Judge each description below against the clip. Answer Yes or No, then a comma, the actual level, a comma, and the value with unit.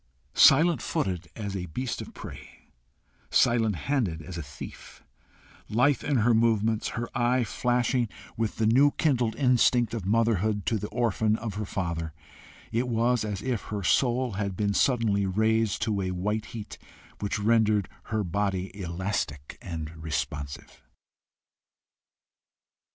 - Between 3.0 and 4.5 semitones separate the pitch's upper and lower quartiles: Yes, average, 3.6 semitones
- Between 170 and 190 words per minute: No, average, 140 wpm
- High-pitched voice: No, low, 110 Hz